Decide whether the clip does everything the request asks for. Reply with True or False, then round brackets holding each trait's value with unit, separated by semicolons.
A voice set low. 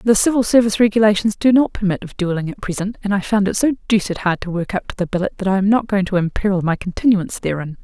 False (200 Hz)